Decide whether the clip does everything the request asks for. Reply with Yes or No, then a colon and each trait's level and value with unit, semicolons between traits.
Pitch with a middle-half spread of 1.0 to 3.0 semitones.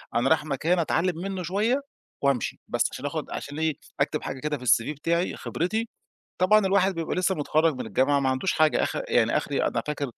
No: average, 4.6 semitones